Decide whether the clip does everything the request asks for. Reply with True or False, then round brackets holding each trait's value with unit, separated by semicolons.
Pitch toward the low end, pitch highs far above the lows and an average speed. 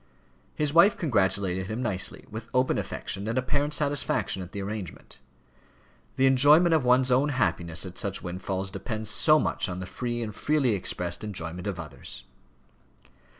True (110 Hz; 5.8 semitones; 155 wpm)